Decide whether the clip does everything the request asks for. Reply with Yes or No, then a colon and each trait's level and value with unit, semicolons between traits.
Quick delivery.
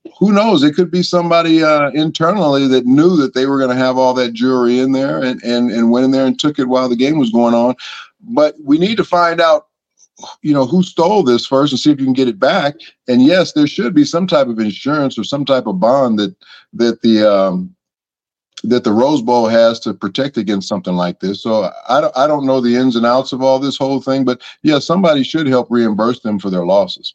Yes: fast, 240 wpm